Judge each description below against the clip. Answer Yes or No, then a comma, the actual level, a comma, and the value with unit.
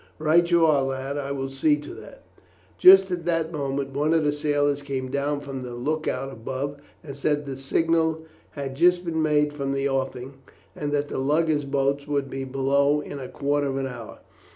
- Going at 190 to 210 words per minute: Yes, fast, 205 wpm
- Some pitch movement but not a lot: No, narrow, 2.1 semitones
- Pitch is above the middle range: No, medium, 145 Hz